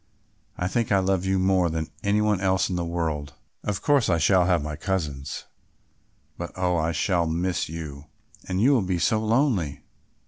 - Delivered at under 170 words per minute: No, average, 185 wpm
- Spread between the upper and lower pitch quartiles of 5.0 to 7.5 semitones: No, average, 3.2 semitones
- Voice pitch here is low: Yes, very low, 90 Hz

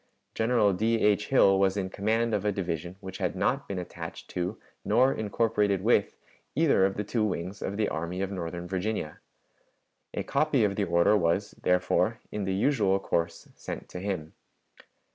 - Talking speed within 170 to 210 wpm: Yes, average, 175 wpm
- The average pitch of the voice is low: Yes, low, 100 Hz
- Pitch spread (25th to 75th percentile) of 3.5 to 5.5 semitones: No, average, 2.9 semitones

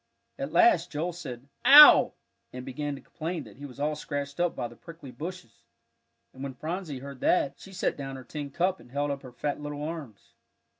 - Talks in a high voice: No, medium, 145 Hz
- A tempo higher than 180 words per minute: Yes, fast, 205 wpm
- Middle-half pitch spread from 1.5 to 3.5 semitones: No, average, 3.9 semitones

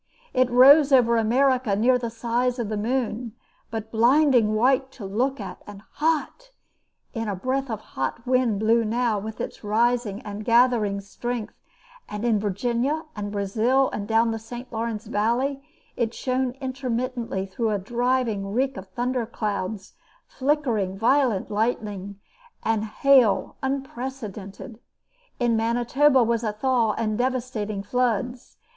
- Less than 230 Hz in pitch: No, high, 235 Hz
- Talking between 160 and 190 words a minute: No, average, 140 wpm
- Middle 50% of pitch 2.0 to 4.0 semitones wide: Yes, average, 3.2 semitones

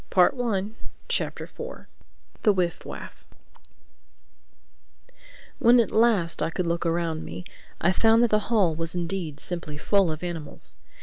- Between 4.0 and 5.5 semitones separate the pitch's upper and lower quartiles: Yes, average, 4.5 semitones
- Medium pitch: Yes, medium, 180 Hz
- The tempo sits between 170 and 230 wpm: No, slow, 135 wpm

